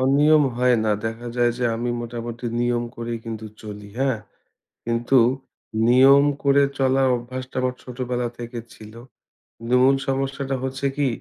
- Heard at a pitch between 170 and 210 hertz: No, low, 125 Hz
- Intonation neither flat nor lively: No, narrow, 2.2 semitones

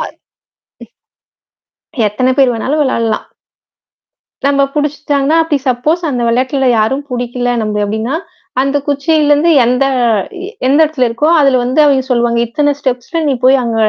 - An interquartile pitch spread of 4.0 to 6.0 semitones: No, average, 3.1 semitones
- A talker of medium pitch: No, very high, 265 Hz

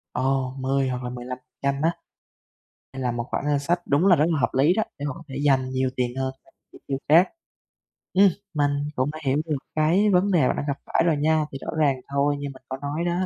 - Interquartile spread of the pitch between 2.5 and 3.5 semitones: Yes, average, 3.1 semitones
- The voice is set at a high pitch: No, medium, 140 Hz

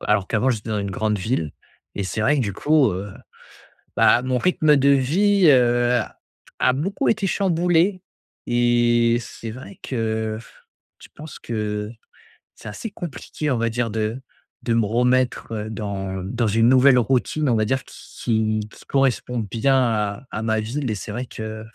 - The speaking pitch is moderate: No, low, 120 Hz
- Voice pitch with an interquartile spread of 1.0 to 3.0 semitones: No, average, 3.7 semitones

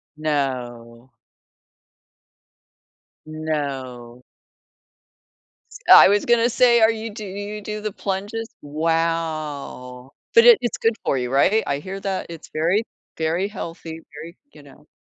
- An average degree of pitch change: No, wide, 6.8 semitones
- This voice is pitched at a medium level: Yes, medium, 165 Hz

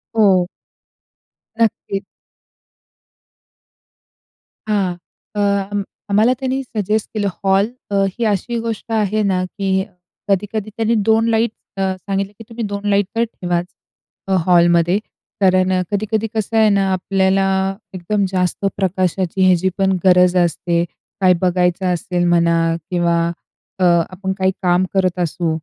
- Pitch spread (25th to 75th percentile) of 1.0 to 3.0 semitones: Yes, narrow, 2.5 semitones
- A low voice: No, high, 190 Hz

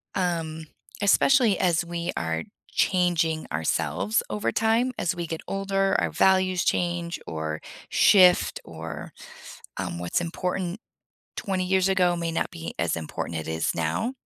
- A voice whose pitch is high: No, medium, 175 Hz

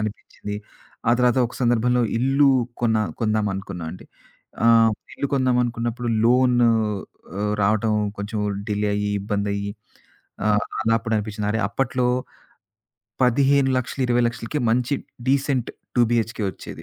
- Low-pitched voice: Yes, low, 115 Hz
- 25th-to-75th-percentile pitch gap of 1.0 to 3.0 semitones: Yes, narrow, 2.6 semitones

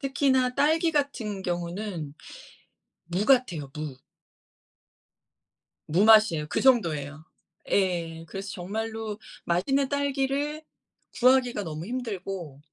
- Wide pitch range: Yes, wide, 7.5 semitones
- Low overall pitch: No, high, 210 Hz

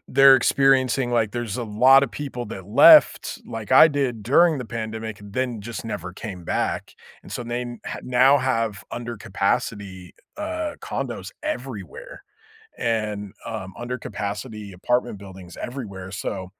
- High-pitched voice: No, low, 115 Hz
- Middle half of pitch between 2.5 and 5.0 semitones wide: Yes, average, 4.1 semitones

